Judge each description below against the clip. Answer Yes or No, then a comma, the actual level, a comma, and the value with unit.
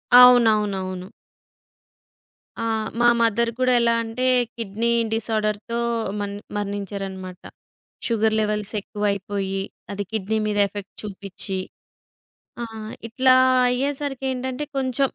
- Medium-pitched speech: No, high, 215 Hz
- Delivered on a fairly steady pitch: No, average, 3.1 semitones